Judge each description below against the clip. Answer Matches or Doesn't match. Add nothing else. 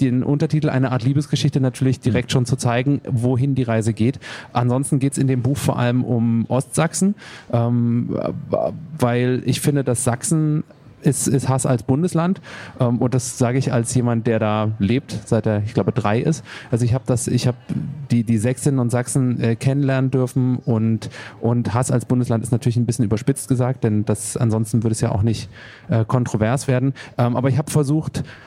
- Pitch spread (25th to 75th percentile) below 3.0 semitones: Matches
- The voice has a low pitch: Matches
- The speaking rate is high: Matches